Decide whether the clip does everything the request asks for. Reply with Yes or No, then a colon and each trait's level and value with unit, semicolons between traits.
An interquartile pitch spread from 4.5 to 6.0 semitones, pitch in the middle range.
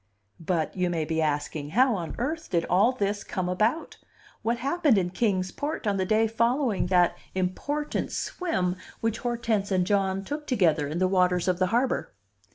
No: average, 4.9 semitones; high, 195 Hz